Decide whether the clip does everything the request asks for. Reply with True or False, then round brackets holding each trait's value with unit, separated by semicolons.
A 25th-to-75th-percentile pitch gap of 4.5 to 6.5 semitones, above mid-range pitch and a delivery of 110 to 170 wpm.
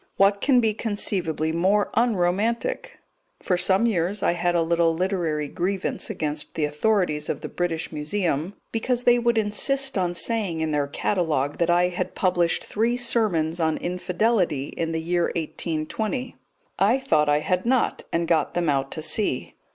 False (4.8 semitones; 175 Hz; 165 wpm)